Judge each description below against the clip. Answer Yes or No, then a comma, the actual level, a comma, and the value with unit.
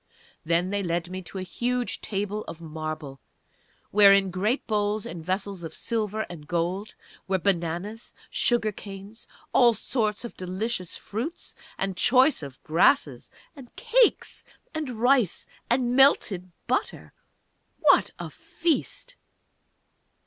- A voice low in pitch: No, high, 205 Hz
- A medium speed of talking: No, slow, 125 wpm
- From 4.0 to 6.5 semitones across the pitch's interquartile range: Yes, average, 5.0 semitones